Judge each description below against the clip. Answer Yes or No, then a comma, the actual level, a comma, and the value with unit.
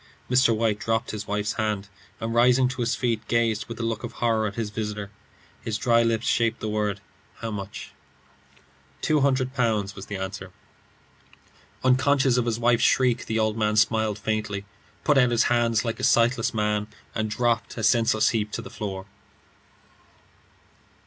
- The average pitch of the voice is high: No, low, 115 Hz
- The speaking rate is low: No, average, 170 wpm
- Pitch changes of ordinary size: No, narrow, 2.0 semitones